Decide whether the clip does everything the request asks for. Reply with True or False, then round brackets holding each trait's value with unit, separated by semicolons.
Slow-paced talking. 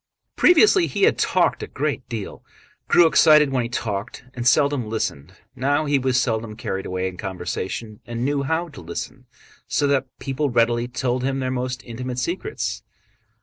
False (170 wpm)